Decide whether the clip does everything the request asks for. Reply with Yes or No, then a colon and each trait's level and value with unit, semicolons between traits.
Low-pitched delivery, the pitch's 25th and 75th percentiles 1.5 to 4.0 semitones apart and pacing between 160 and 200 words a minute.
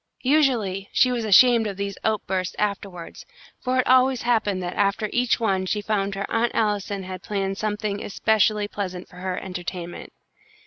No: high, 205 Hz; average, 2.8 semitones; average, 165 wpm